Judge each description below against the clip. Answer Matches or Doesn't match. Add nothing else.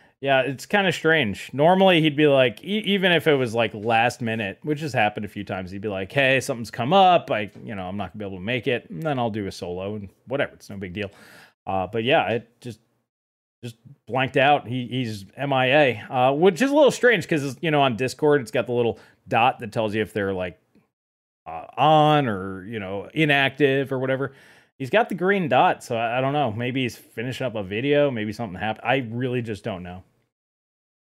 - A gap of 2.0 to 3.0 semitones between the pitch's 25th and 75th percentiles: Doesn't match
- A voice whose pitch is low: Matches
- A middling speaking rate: Doesn't match